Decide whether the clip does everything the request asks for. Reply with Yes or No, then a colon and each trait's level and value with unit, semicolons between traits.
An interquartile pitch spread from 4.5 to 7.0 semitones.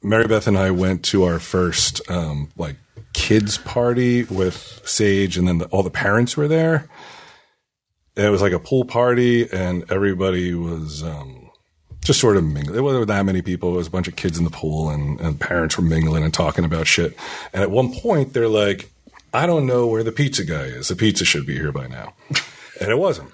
Yes: average, 5.1 semitones